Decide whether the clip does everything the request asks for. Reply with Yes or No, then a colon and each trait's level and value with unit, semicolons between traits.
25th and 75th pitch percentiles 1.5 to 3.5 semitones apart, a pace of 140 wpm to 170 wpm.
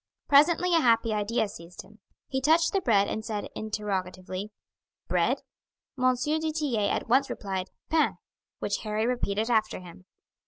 No: wide, 5.5 semitones; average, 150 wpm